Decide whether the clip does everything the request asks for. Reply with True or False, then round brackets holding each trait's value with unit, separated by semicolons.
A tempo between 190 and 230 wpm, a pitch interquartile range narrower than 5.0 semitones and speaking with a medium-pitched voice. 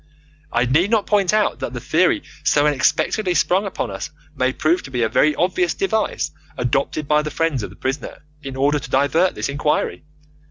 False (195 wpm; 5.3 semitones; 150 Hz)